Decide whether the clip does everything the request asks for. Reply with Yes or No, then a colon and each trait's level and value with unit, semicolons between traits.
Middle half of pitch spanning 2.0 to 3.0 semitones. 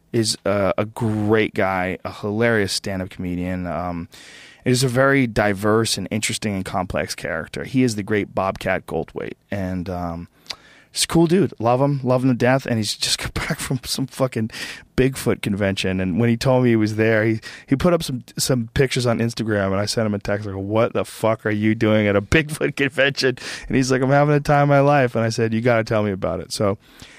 No: average, 4.2 semitones